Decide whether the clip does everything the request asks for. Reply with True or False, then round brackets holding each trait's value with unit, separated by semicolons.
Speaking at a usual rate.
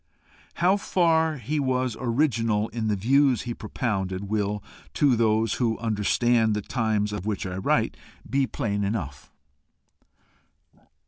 False (130 wpm)